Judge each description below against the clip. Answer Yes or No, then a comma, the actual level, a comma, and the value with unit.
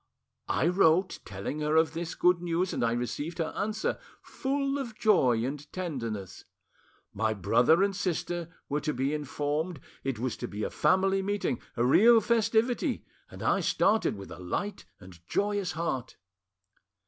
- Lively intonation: Yes, wide, 7.3 semitones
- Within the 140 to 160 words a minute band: Yes, average, 155 wpm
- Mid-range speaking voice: Yes, medium, 165 Hz